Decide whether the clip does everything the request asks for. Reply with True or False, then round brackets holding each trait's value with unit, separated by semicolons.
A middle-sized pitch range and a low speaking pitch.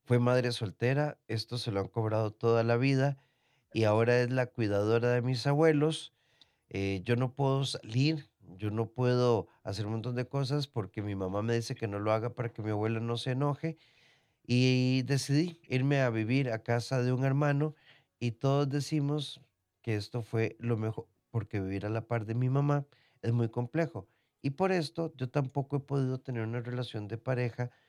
True (3.5 semitones; 125 Hz)